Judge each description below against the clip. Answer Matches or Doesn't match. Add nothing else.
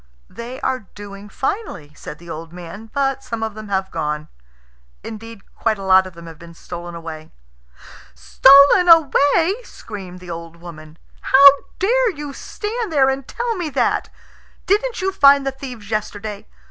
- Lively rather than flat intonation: Matches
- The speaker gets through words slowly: Doesn't match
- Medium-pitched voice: Doesn't match